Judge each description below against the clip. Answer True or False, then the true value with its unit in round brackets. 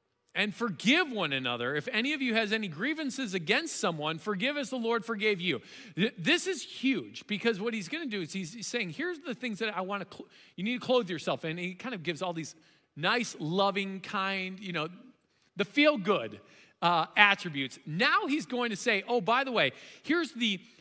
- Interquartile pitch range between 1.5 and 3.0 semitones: False (5.1 semitones)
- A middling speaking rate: False (210 wpm)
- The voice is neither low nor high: False (215 Hz)